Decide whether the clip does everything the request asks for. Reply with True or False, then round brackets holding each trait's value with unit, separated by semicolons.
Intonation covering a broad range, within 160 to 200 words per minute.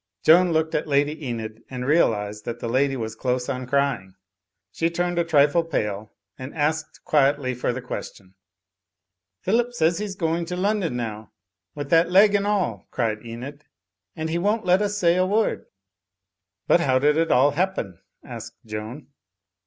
True (5.8 semitones; 170 wpm)